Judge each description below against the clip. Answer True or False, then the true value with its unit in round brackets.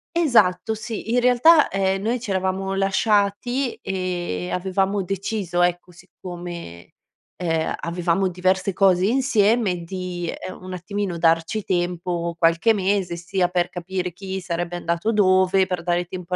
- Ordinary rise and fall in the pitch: False (2.3 semitones)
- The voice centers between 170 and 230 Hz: True (185 Hz)